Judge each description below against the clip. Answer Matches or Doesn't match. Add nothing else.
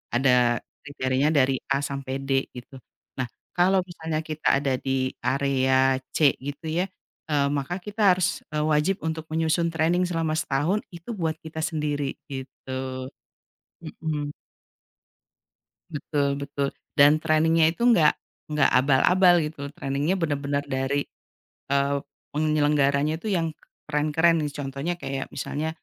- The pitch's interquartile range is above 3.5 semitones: Doesn't match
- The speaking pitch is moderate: Matches